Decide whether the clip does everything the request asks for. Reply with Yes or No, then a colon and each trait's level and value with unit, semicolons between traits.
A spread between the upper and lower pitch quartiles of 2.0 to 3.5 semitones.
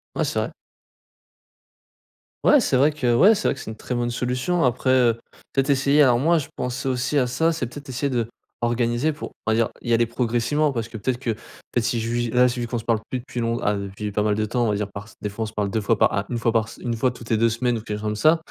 Yes: narrow, 2.6 semitones